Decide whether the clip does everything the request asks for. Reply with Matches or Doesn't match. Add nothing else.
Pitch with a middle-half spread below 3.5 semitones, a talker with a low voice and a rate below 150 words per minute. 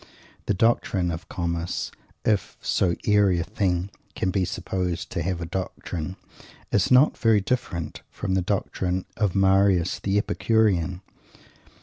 Matches